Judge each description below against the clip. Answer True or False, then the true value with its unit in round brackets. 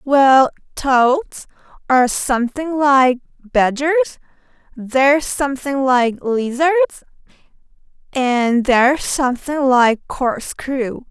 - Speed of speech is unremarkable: False (70 wpm)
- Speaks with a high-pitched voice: True (270 Hz)